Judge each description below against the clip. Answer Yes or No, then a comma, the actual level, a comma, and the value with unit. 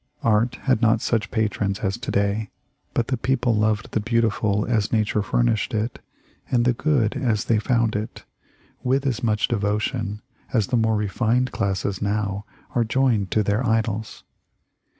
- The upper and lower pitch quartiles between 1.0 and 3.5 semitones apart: Yes, narrow, 2.4 semitones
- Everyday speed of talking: Yes, average, 165 wpm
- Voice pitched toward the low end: Yes, low, 110 Hz